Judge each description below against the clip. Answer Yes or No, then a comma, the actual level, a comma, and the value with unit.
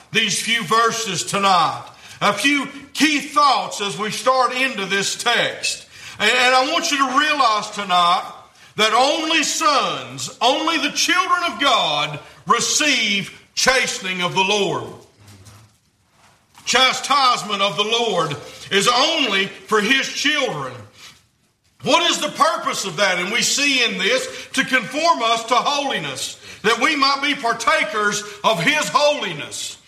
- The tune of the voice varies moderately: No, wide, 6.4 semitones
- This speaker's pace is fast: No, slow, 135 wpm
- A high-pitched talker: Yes, high, 235 Hz